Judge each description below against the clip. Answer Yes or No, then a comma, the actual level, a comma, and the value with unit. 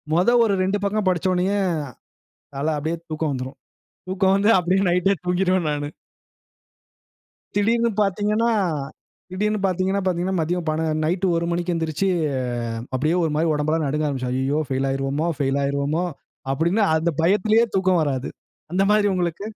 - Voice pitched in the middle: Yes, medium, 175 Hz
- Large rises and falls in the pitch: No, average, 4.1 semitones